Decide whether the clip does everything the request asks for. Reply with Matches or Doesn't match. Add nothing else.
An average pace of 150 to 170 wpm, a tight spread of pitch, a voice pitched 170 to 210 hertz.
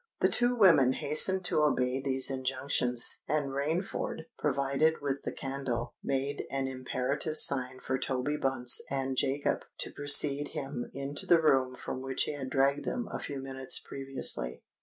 Doesn't match